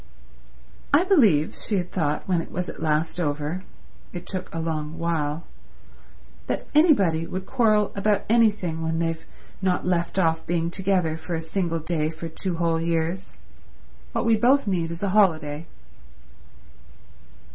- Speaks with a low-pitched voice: No, medium, 170 Hz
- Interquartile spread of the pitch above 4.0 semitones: No, average, 3.1 semitones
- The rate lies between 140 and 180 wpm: Yes, average, 145 wpm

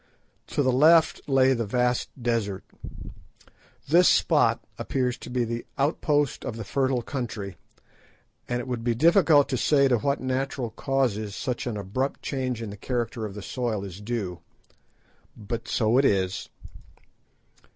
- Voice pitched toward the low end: Yes, low, 120 Hz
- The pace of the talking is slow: No, average, 150 wpm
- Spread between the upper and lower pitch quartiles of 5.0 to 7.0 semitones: No, average, 3.6 semitones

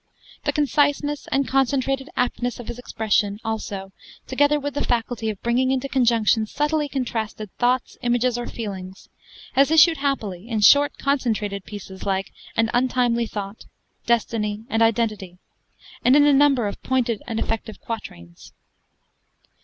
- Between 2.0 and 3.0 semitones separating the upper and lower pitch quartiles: No, average, 4.0 semitones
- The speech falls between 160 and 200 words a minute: No, average, 140 wpm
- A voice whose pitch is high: Yes, high, 235 Hz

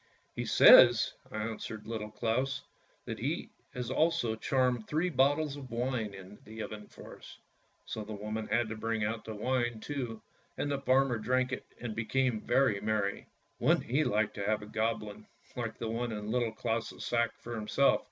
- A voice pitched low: Yes, low, 115 Hz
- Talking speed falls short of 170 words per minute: No, average, 185 wpm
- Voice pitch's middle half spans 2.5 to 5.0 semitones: Yes, average, 3.0 semitones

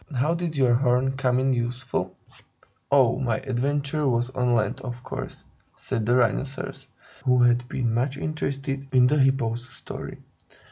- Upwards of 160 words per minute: No, average, 150 wpm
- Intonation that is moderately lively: No, narrow, 2.0 semitones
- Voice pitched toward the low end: Yes, low, 130 Hz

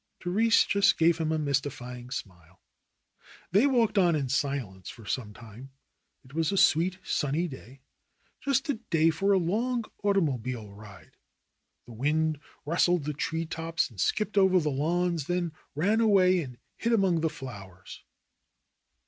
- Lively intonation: Yes, wide, 6.3 semitones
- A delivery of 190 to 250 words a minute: No, average, 150 wpm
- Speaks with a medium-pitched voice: Yes, medium, 160 Hz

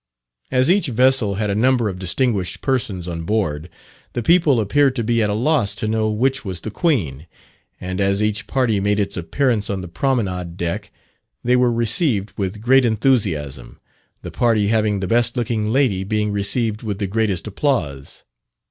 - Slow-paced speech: No, average, 175 wpm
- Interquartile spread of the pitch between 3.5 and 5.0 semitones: Yes, average, 4.2 semitones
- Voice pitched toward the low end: Yes, low, 110 Hz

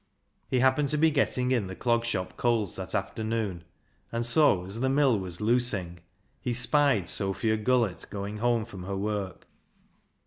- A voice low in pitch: Yes, low, 115 Hz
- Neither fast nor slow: Yes, average, 165 wpm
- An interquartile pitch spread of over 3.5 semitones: Yes, average, 4.2 semitones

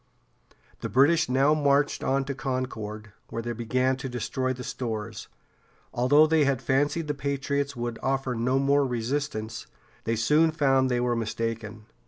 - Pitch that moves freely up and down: No, average, 3.3 semitones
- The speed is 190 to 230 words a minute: No, average, 155 wpm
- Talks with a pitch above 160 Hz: No, low, 130 Hz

